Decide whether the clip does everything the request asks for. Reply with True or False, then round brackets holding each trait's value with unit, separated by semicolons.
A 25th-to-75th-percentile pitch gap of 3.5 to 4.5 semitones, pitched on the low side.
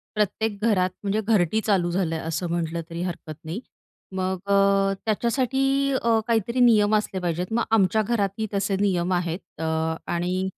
False (3.9 semitones; 195 Hz)